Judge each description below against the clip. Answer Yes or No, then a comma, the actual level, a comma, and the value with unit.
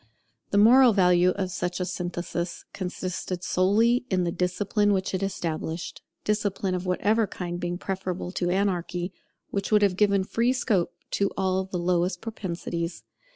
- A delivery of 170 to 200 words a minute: No, average, 155 wpm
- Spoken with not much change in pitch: Yes, narrow, 2.2 semitones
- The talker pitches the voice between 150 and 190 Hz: Yes, medium, 185 Hz